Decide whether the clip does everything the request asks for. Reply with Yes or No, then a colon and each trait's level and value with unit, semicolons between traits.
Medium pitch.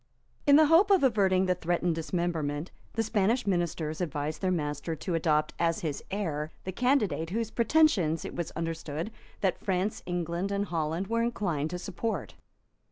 Yes: medium, 175 Hz